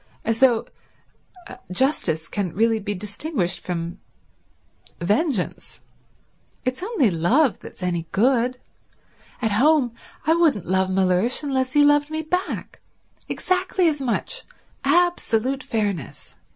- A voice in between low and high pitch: No, high, 240 Hz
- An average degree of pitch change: No, wide, 7.6 semitones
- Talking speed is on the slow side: Yes, slow, 110 wpm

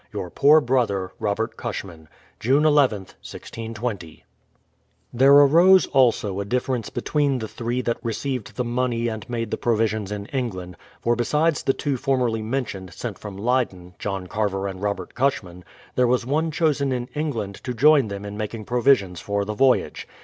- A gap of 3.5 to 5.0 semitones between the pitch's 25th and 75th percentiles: Yes, average, 4.6 semitones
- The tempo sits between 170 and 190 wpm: Yes, average, 175 wpm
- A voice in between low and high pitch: No, low, 115 Hz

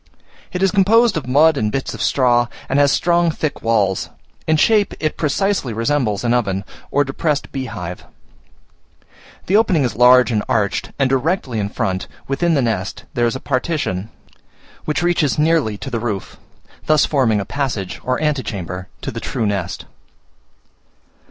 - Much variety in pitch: Yes, wide, 6.0 semitones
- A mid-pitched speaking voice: No, low, 130 Hz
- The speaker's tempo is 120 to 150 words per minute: No, average, 160 wpm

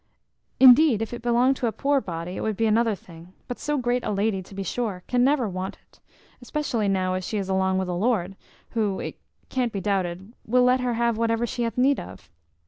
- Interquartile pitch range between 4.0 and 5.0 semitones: Yes, average, 4.5 semitones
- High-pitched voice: Yes, high, 225 Hz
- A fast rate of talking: Yes, fast, 225 wpm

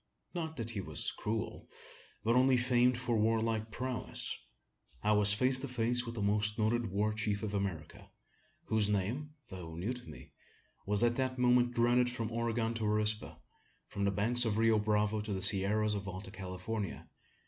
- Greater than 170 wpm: Yes, average, 180 wpm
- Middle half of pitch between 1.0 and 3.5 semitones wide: Yes, average, 2.8 semitones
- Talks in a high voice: No, low, 110 Hz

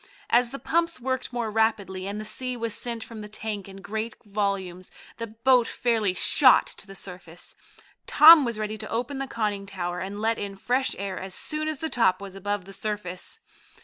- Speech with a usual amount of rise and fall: Yes, average, 3.7 semitones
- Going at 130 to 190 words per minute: No, average, 200 wpm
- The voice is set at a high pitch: Yes, high, 215 Hz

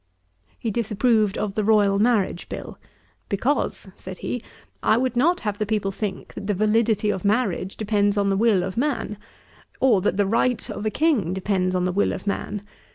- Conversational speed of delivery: Yes, average, 190 wpm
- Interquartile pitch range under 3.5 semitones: Yes, narrow, 2.6 semitones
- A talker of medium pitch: No, high, 210 Hz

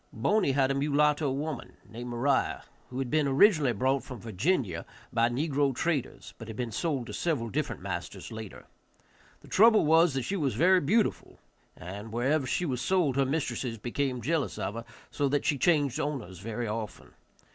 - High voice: No, low, 135 Hz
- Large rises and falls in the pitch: No, average, 4.4 semitones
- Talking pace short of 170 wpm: No, average, 180 wpm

